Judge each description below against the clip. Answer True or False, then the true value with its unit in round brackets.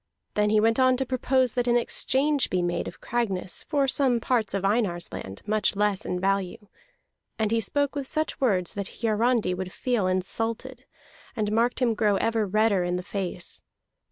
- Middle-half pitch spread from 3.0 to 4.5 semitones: True (4.1 semitones)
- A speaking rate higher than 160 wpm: True (185 wpm)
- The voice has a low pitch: False (220 Hz)